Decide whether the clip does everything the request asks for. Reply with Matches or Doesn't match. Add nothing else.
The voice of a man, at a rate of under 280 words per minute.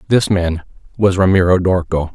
Matches